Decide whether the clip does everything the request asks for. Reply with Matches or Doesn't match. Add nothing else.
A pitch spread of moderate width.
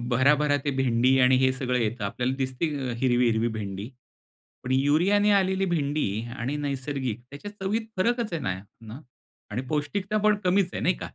Doesn't match